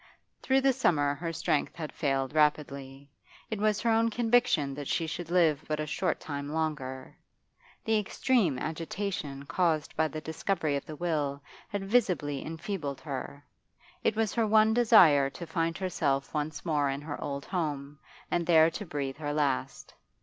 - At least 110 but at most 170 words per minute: Yes, average, 165 wpm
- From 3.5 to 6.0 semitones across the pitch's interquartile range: Yes, average, 4.7 semitones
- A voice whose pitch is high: No, medium, 155 Hz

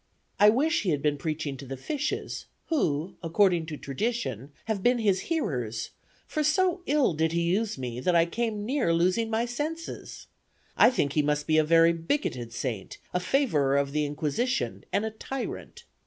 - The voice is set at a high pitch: No, medium, 170 Hz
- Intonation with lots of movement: Yes, wide, 8.5 semitones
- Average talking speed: Yes, average, 180 wpm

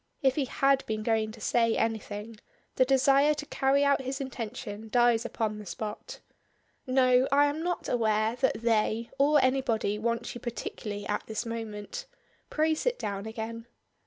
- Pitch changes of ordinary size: Yes, average, 3.8 semitones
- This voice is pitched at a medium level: No, high, 235 Hz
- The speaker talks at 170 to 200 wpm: No, average, 160 wpm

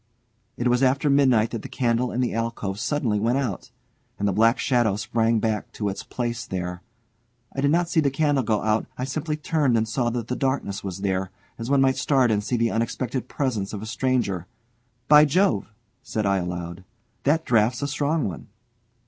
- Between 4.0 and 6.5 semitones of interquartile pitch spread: Yes, average, 4.3 semitones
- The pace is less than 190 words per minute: No, average, 200 wpm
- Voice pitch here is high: No, low, 120 Hz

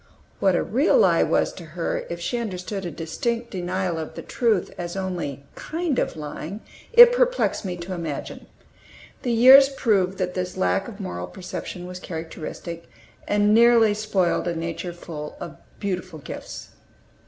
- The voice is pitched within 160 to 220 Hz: Yes, medium, 185 Hz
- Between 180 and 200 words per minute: No, average, 160 wpm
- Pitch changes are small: No, average, 4.7 semitones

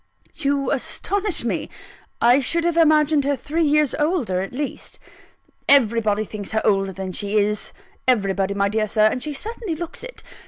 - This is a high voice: Yes, very high, 255 Hz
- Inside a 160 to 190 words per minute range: Yes, average, 165 wpm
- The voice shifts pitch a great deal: Yes, wide, 6.5 semitones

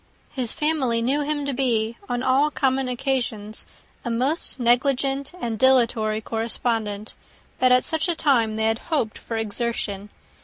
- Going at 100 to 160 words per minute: Yes, average, 150 wpm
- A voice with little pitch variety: No, average, 3.4 semitones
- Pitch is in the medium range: No, high, 245 Hz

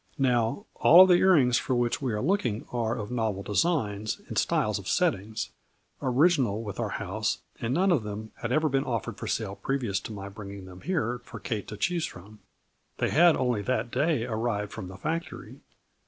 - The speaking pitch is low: Yes, low, 120 Hz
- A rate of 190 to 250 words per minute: Yes, average, 200 wpm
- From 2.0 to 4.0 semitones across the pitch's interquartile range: No, average, 5.1 semitones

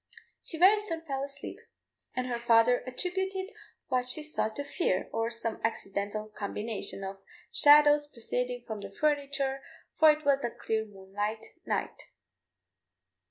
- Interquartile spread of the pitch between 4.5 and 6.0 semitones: Yes, average, 5.2 semitones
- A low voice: No, very high, 250 Hz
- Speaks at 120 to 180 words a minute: Yes, average, 140 wpm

